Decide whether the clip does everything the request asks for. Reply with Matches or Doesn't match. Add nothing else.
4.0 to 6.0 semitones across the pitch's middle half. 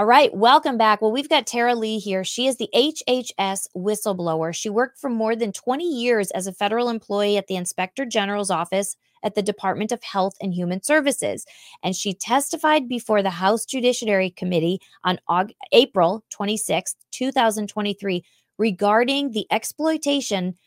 Matches